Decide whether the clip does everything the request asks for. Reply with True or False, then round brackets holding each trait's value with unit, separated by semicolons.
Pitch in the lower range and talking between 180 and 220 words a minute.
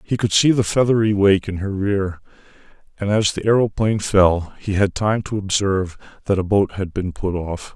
True (100 Hz; 200 wpm)